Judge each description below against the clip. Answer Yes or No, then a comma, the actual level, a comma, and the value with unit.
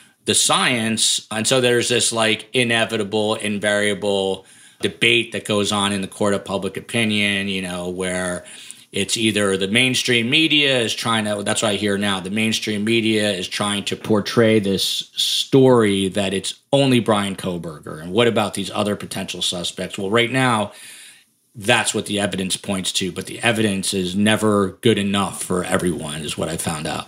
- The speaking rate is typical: Yes, average, 175 wpm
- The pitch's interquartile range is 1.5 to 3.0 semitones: Yes, average, 2.7 semitones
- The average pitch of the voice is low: Yes, low, 105 Hz